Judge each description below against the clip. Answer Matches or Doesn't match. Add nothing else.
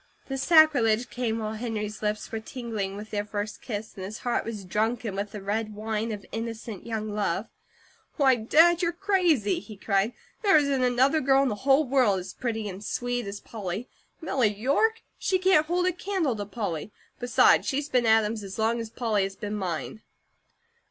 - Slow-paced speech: Doesn't match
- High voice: Matches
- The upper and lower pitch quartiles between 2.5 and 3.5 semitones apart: Doesn't match